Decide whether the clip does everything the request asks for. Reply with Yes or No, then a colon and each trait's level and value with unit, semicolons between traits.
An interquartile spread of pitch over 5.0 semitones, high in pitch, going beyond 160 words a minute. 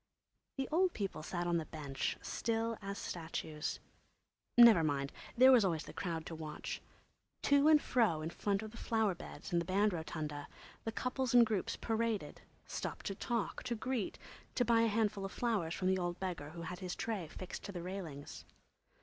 Yes: wide, 5.4 semitones; high, 195 Hz; average, 190 wpm